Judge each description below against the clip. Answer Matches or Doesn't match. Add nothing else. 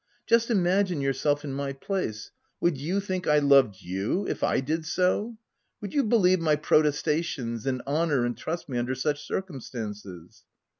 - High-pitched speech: Doesn't match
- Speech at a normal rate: Matches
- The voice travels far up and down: Matches